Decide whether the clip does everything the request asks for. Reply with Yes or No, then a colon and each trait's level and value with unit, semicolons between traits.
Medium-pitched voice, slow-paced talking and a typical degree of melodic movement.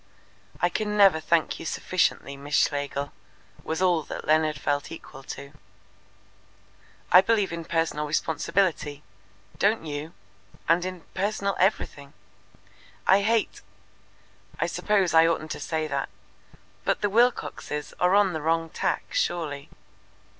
Yes: medium, 165 Hz; slow, 130 wpm; average, 4.4 semitones